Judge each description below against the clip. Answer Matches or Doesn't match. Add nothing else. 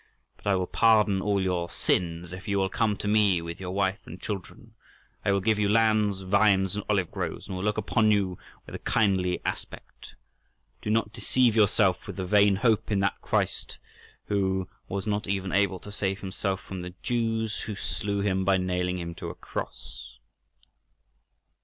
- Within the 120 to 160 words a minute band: Doesn't match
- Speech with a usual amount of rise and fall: Doesn't match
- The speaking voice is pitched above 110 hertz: Doesn't match